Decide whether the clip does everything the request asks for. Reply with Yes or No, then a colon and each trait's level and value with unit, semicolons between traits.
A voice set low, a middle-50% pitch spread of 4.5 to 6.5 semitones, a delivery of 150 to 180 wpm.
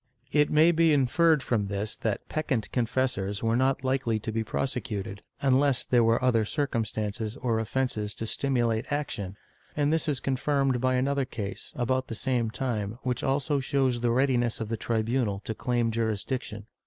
No: low, 125 Hz; average, 3.3 semitones; average, 170 wpm